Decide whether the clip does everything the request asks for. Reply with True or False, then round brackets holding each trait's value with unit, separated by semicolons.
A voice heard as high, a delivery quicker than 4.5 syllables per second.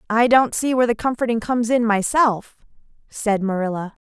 True (225 Hz; 5.5 syllables/s)